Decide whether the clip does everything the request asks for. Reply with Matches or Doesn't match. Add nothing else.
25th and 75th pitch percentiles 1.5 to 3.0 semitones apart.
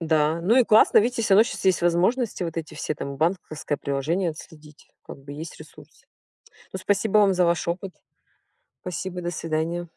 Doesn't match